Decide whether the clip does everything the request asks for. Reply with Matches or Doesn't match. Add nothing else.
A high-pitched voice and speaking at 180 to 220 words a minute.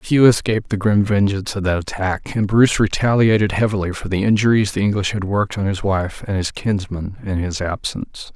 Doesn't match